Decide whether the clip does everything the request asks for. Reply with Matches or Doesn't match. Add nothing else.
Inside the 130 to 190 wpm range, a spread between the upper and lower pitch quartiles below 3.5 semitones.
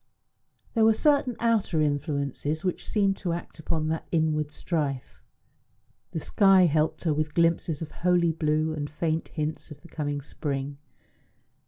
Matches